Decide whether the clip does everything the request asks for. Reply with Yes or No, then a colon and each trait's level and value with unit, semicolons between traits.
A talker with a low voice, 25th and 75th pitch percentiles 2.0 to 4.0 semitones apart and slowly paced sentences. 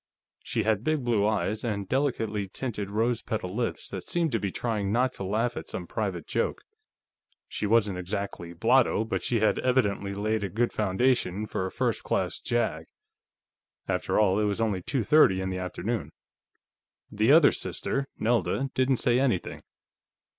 No: low, 110 Hz; average, 3.5 semitones; average, 170 wpm